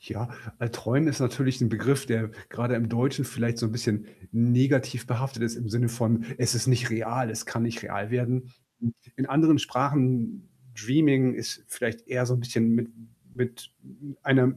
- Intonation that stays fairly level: Yes, narrow, 2.1 semitones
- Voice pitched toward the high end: No, low, 120 Hz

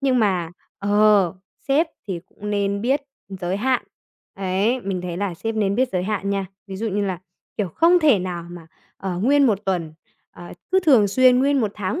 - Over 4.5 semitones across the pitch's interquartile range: Yes, average, 5.0 semitones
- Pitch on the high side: Yes, high, 200 Hz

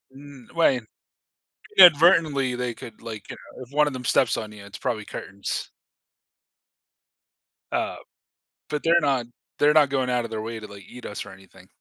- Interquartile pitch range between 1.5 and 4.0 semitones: No, average, 4.9 semitones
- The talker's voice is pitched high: No, low, 125 Hz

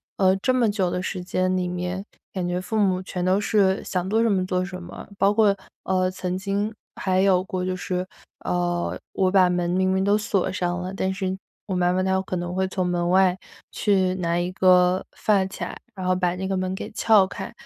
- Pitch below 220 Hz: Yes, medium, 185 Hz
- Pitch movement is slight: Yes, narrow, 1.1 semitones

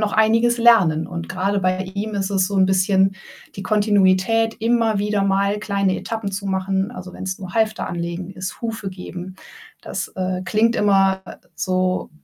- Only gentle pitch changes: Yes, narrow, 2.3 semitones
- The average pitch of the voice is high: Yes, high, 195 Hz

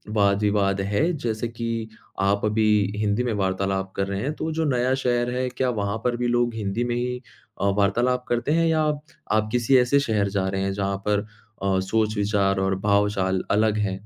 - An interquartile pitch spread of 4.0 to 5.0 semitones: No, average, 3.5 semitones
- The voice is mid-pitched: No, low, 110 Hz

